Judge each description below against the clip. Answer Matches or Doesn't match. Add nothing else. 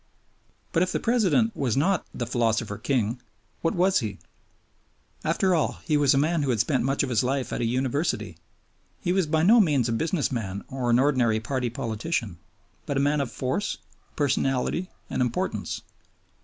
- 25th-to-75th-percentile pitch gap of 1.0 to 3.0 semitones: Doesn't match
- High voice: Doesn't match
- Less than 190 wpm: Matches